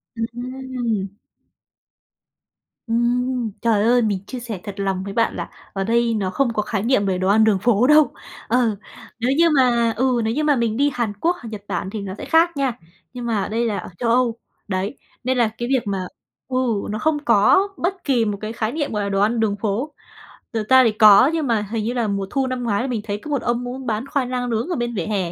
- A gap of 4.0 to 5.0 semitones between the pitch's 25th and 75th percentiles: No, average, 3.4 semitones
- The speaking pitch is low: No, high, 235 Hz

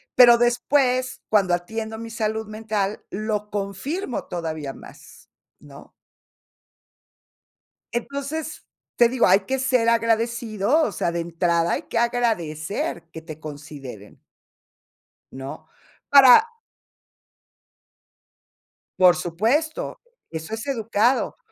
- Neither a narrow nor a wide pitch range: No, wide, 5.7 semitones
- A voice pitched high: Yes, high, 220 Hz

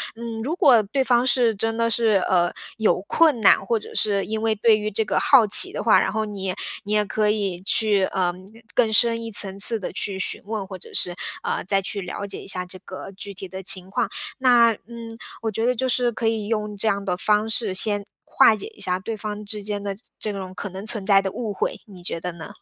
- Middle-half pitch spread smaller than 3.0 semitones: Yes, narrow, 2.6 semitones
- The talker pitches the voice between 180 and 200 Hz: No, high, 210 Hz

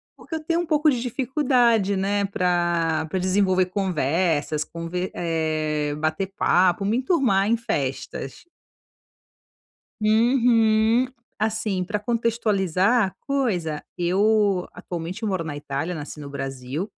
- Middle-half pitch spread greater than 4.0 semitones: Yes, wide, 5.4 semitones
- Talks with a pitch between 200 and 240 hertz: No, high, 190 Hz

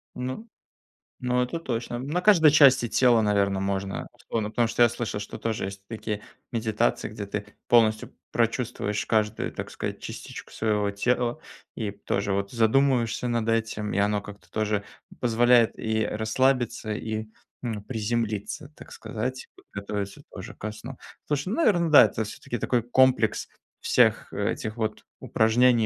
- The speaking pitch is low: Yes, low, 110 Hz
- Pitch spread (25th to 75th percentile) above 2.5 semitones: Yes, average, 2.9 semitones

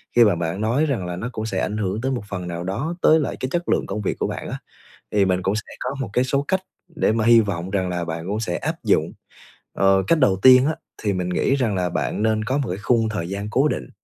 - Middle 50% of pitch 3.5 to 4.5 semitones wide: No, average, 5.3 semitones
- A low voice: Yes, low, 105 Hz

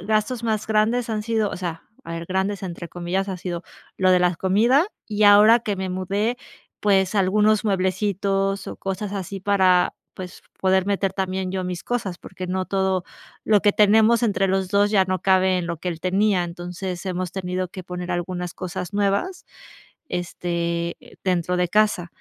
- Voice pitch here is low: No, high, 190 Hz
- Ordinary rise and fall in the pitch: No, narrow, 2.3 semitones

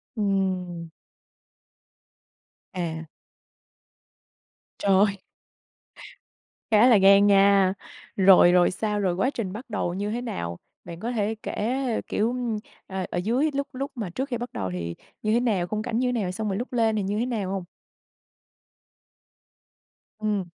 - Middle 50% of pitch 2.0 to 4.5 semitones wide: Yes, average, 3.8 semitones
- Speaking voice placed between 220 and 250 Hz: No, high, 205 Hz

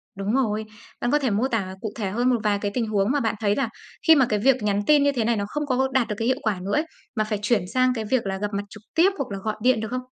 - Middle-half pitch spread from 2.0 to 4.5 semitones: Yes, average, 3.7 semitones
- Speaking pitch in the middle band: No, high, 225 Hz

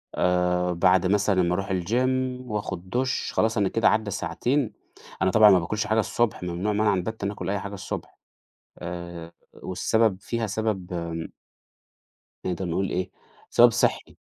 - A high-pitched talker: No, very low, 95 Hz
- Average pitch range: Yes, average, 3.6 semitones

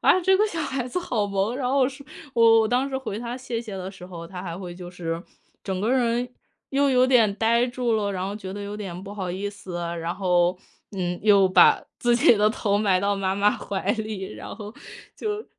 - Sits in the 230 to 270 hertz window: No, high, 210 Hz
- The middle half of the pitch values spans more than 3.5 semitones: Yes, average, 4.4 semitones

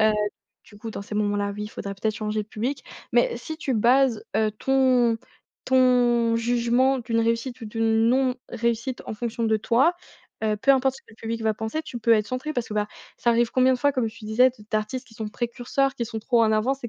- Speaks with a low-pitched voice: No, high, 230 Hz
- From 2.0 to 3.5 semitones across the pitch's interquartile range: Yes, average, 2.8 semitones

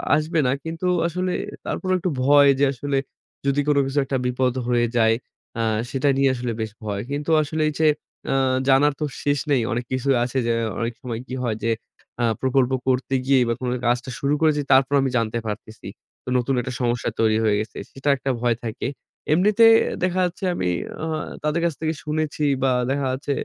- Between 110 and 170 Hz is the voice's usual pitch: Yes, low, 135 Hz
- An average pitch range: Yes, average, 3.8 semitones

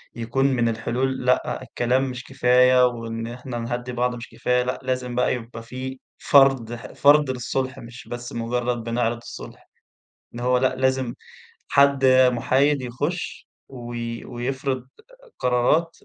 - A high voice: No, low, 125 Hz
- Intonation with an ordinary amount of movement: No, narrow, 1.7 semitones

